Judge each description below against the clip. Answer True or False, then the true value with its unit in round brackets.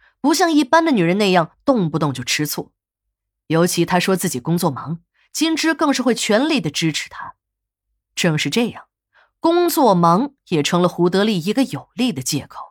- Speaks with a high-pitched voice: False (180 Hz)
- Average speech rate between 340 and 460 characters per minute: False (260 characters per minute)